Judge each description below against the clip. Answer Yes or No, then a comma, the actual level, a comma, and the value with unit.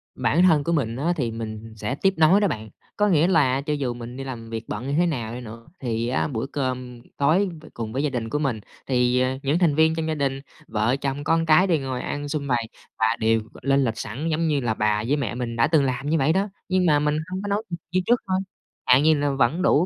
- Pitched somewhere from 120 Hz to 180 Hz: Yes, low, 135 Hz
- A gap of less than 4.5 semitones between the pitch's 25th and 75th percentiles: No, average, 4.9 semitones